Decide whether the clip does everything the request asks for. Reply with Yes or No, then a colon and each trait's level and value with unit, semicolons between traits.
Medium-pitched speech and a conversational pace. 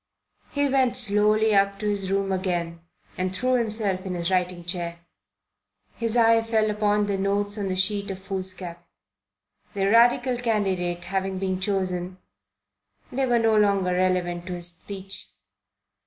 No: high, 195 Hz; average, 150 wpm